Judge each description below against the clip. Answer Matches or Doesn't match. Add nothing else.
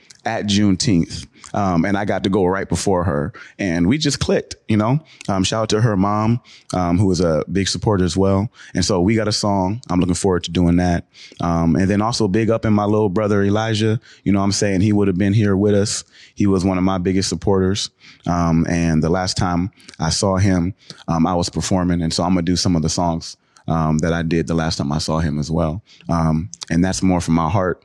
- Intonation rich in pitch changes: Doesn't match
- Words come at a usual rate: Doesn't match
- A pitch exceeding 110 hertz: Doesn't match